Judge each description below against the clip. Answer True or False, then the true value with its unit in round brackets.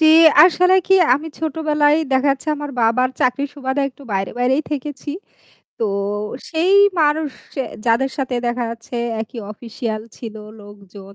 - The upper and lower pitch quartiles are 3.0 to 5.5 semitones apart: True (4.4 semitones)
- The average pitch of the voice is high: True (265 Hz)